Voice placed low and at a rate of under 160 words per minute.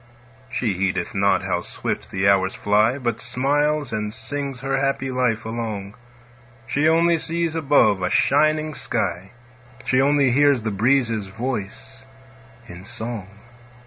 Yes: low, 120 Hz; slow, 135 wpm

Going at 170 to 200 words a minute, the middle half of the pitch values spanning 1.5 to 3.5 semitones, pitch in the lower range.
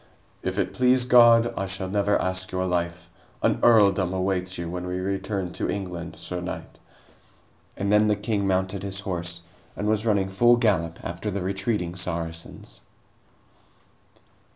No: average, 155 wpm; narrow, 2.5 semitones; very low, 95 Hz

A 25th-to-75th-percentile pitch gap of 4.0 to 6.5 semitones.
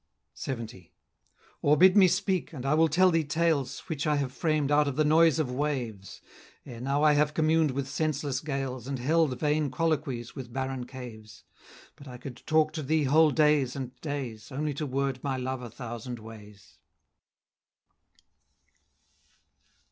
No: average, 3.4 semitones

